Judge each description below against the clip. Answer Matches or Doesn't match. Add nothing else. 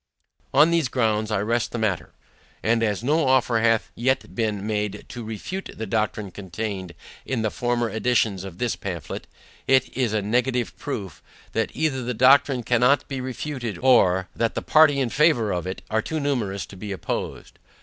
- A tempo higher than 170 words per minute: Matches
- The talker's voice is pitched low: Matches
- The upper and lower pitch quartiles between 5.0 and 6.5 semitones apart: Doesn't match